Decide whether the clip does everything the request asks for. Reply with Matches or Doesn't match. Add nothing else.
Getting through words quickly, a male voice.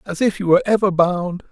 Matches